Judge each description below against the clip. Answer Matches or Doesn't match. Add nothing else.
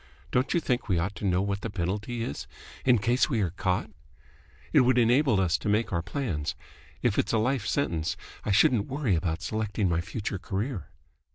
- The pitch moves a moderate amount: Matches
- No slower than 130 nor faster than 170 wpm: Doesn't match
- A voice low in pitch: Matches